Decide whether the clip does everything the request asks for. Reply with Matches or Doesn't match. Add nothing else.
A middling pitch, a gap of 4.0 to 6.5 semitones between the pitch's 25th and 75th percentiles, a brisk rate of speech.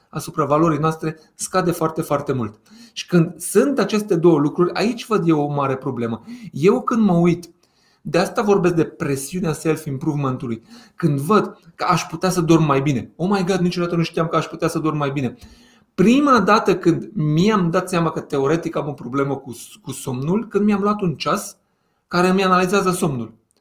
Matches